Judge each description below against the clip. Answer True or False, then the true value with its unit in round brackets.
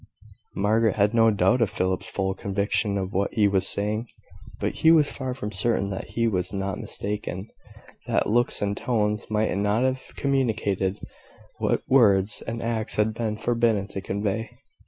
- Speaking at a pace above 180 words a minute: False (165 wpm)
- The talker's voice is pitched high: False (105 Hz)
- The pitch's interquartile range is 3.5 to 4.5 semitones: False (2.6 semitones)